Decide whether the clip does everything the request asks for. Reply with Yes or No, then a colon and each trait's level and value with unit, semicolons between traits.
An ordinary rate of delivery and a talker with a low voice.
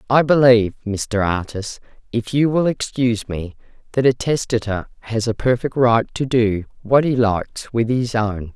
Yes: average, 170 wpm; low, 115 Hz